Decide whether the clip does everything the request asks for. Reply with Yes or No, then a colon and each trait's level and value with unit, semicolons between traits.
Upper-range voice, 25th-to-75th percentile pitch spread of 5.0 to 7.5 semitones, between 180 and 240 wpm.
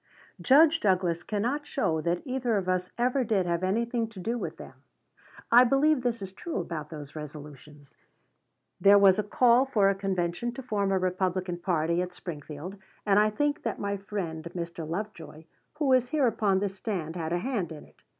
Yes: high, 195 Hz; wide, 5.5 semitones; average, 190 wpm